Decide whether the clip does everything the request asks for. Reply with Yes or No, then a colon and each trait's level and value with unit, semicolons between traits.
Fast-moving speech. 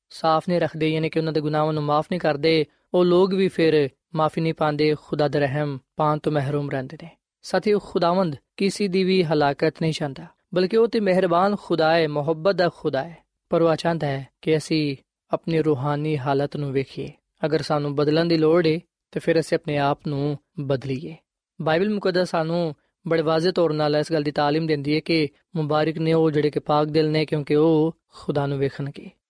Yes: fast, 175 wpm